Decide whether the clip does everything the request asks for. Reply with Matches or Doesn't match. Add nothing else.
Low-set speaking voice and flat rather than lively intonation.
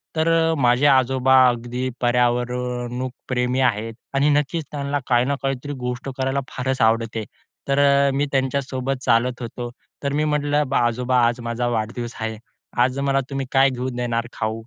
Matches